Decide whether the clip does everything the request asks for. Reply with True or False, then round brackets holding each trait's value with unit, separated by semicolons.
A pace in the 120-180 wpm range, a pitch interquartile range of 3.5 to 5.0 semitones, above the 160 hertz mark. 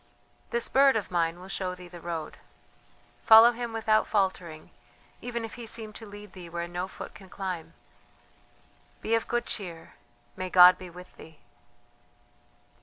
True (160 wpm; 4.2 semitones; 185 Hz)